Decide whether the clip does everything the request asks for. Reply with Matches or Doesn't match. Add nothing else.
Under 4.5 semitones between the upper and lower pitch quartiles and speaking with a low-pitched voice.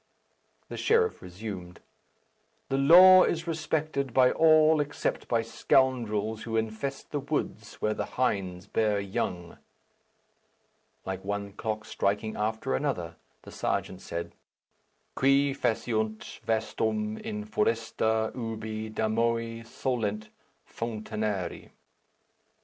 Matches